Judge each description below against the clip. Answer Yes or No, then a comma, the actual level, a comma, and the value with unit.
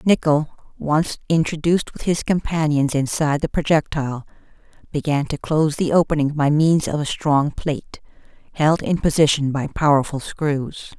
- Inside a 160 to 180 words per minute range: No, average, 140 wpm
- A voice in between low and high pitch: Yes, medium, 150 Hz